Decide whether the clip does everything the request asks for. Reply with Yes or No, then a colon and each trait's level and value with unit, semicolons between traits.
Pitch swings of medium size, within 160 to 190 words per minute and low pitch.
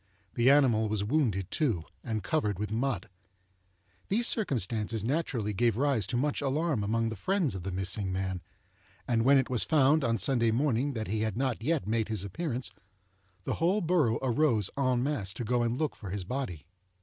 Yes: average, 4.9 semitones; average, 185 wpm; low, 120 Hz